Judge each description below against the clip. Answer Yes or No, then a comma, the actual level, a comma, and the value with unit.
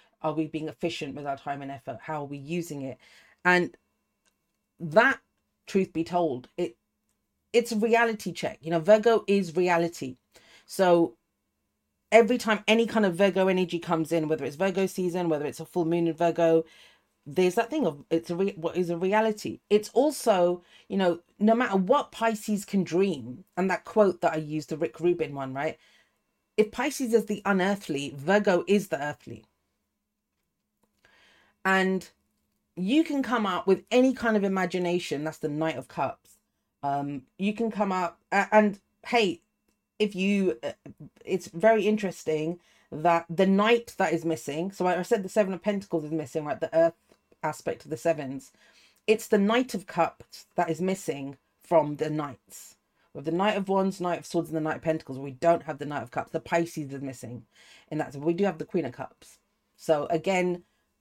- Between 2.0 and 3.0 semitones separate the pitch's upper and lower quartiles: No, average, 4.2 semitones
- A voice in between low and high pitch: Yes, medium, 175 Hz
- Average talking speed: Yes, average, 185 wpm